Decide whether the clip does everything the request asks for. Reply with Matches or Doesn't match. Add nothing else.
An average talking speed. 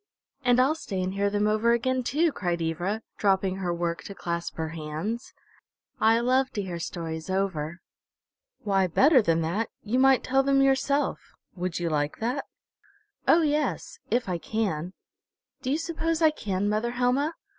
Matches